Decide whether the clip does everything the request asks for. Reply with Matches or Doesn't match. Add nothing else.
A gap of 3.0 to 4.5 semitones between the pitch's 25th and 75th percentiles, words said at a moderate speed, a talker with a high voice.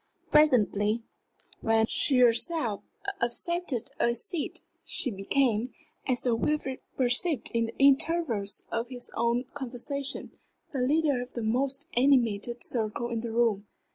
Doesn't match